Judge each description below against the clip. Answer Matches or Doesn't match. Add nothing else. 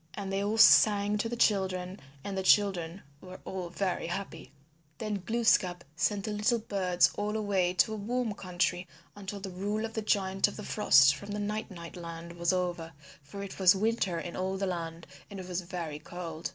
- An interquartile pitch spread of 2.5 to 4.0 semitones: Matches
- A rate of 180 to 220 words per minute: Matches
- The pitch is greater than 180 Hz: Matches